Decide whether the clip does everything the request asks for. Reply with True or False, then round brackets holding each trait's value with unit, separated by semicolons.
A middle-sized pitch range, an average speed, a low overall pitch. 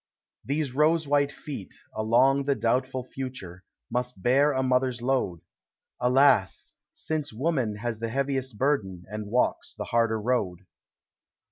False (3.7 semitones; 130 wpm; 125 Hz)